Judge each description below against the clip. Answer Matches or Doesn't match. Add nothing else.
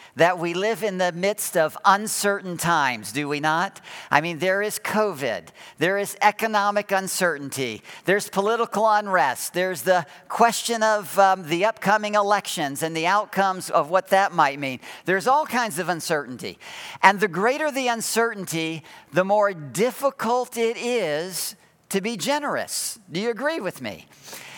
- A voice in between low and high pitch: Doesn't match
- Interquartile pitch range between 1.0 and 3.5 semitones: Doesn't match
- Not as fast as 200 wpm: Matches